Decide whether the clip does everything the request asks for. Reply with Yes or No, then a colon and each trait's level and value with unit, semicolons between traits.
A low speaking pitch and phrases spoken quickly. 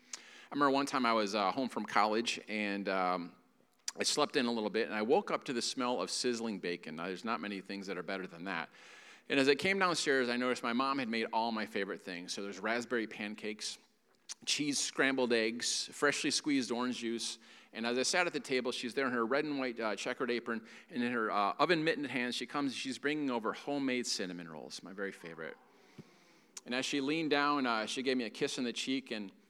Yes: low, 120 Hz; fast, 230 wpm